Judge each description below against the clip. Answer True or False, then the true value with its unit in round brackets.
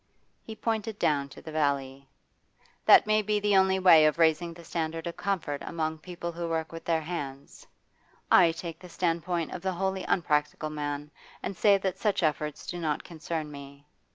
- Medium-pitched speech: True (165 Hz)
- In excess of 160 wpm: True (180 wpm)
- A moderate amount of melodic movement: True (3.3 semitones)